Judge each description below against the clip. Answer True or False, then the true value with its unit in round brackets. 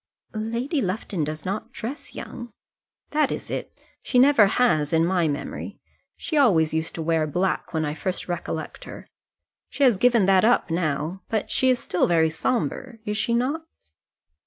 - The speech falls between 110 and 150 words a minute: False (170 wpm)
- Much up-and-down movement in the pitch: True (7.1 semitones)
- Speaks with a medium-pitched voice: False (195 Hz)